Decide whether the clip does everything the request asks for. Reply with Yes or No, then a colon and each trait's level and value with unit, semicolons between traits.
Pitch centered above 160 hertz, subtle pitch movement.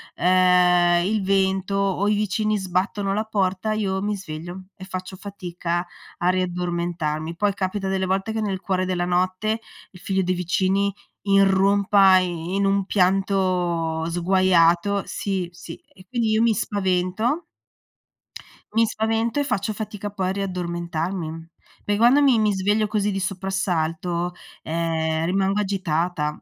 Yes: high, 190 Hz; narrow, 2.3 semitones